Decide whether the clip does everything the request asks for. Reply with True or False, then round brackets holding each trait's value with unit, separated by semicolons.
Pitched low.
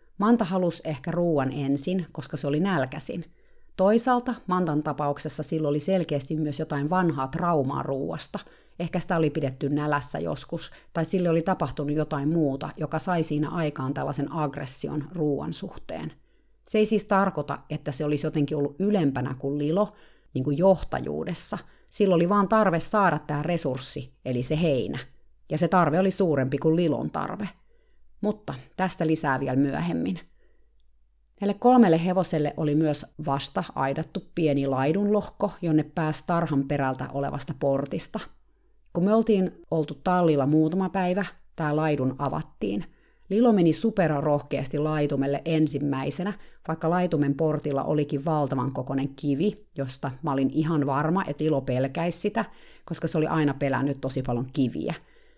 False (155 Hz)